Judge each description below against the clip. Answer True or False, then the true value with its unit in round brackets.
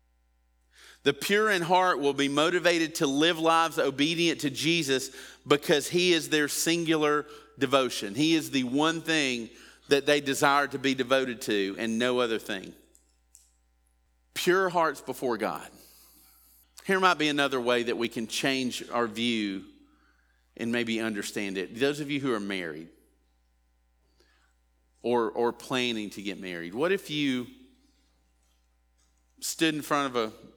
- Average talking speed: True (145 wpm)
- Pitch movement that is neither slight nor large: False (8.7 semitones)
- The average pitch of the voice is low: True (130 Hz)